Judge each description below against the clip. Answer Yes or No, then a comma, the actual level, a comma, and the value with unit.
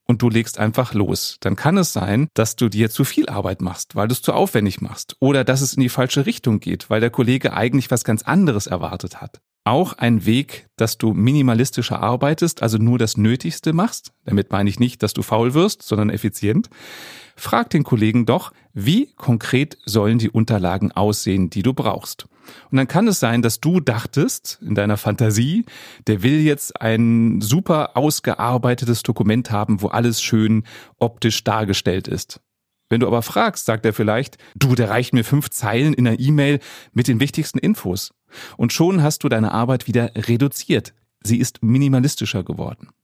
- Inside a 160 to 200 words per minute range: Yes, average, 185 wpm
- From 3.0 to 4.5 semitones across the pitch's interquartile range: Yes, average, 3.9 semitones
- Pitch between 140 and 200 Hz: No, low, 120 Hz